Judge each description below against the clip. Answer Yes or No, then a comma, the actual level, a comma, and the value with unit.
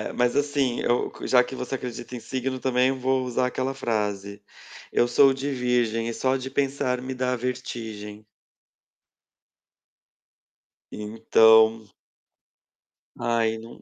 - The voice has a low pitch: Yes, low, 125 Hz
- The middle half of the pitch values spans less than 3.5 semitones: Yes, narrow, 2.6 semitones